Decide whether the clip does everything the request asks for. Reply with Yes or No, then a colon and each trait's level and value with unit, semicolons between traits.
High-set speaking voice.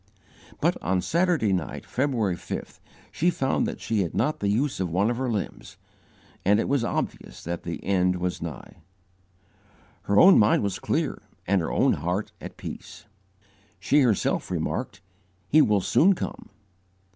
No: low, 100 Hz